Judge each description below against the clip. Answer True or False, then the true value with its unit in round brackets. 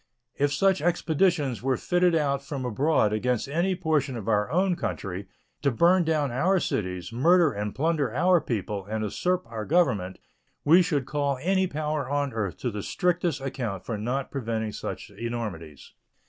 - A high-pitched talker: False (140 Hz)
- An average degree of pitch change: False (7.0 semitones)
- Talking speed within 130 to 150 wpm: False (165 wpm)